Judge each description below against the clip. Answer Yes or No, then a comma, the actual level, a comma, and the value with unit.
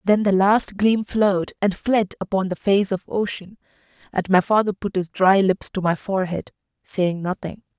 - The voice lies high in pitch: Yes, high, 195 Hz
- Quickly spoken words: No, average, 185 wpm